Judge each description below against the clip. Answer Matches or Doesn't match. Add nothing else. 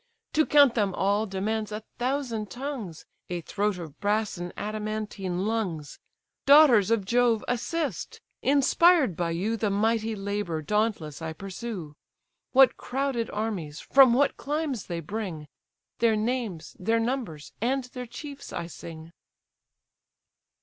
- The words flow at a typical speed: Doesn't match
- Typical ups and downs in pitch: Matches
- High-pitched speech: Matches